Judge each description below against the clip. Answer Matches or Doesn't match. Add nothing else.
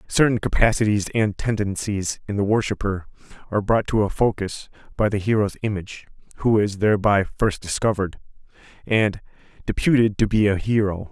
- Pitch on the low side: Matches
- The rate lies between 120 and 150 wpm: Matches